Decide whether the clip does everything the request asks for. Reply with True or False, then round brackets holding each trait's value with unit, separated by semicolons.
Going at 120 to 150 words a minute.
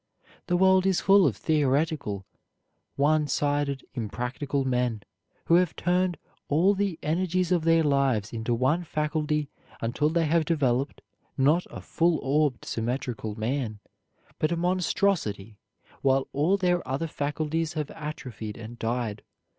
True (135 wpm)